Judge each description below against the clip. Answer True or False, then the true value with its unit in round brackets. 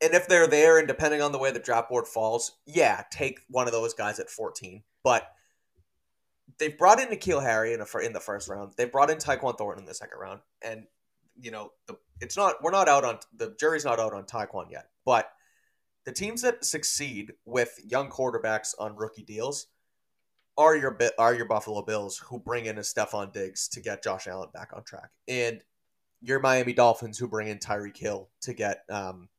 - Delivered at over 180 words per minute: True (205 wpm)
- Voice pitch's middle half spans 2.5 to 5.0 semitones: False (5.5 semitones)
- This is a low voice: True (115 Hz)